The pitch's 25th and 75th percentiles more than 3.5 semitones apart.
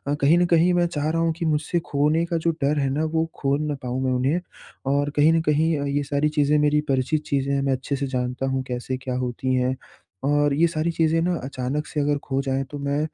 No: average, 2.8 semitones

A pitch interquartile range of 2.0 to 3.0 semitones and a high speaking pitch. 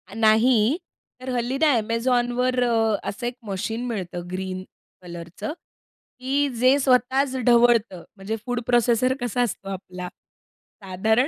No: average, 4.1 semitones; high, 235 Hz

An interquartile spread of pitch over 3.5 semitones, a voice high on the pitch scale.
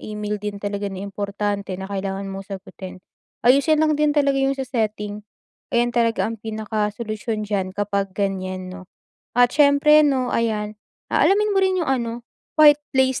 Yes: average, 4.7 semitones; high, 215 Hz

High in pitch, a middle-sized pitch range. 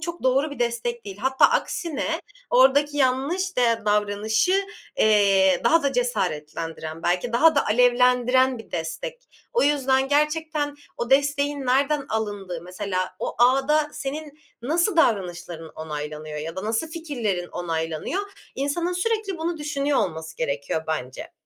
No: very high, 250 Hz; wide, 7.8 semitones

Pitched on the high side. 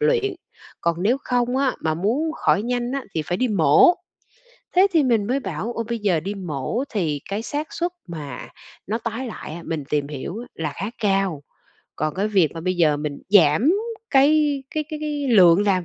Yes: high, 205 Hz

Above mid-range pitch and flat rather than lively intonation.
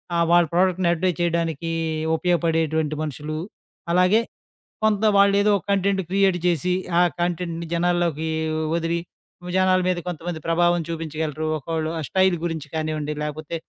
No: medium, 170 Hz; narrow, 2.3 semitones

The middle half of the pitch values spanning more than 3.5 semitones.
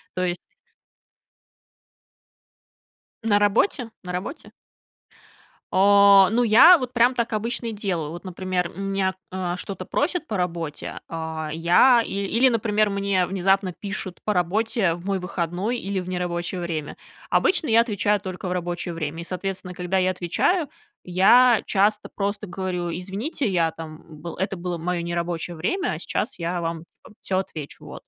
No: average, 3.2 semitones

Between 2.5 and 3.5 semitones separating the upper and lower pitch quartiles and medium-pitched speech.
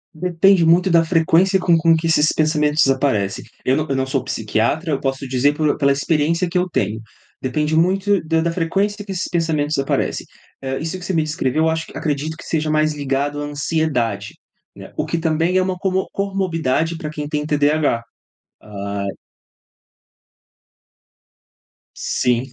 Yes: average, 3.2 semitones; medium, 155 Hz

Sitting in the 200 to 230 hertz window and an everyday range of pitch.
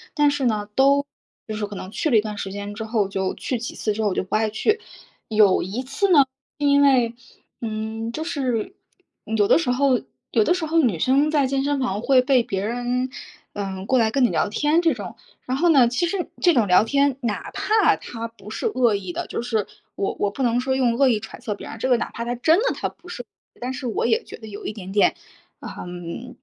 No: high, 240 Hz; average, 4.7 semitones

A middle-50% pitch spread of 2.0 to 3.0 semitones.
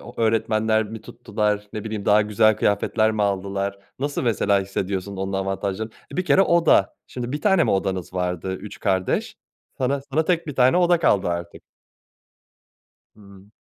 No: average, 4.2 semitones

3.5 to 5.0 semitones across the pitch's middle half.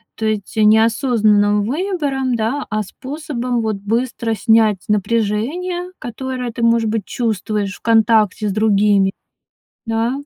No: average, 3.0 semitones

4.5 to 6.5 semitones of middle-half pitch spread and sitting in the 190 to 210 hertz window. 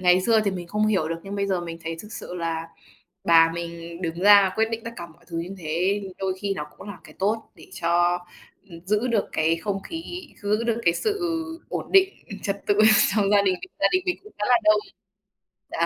No: average, 3.9 semitones; high, 195 Hz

